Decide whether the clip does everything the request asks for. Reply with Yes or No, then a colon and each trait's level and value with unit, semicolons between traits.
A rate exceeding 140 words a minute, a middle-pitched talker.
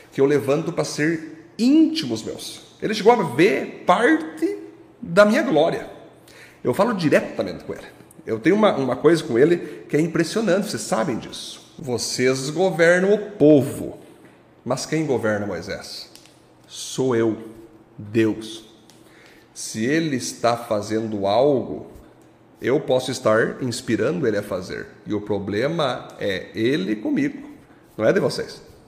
No: average, 135 wpm; medium, 150 Hz